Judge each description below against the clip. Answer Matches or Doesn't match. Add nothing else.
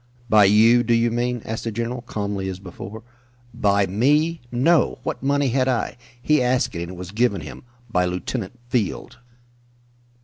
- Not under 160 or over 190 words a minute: Matches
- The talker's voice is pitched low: Matches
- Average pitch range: Matches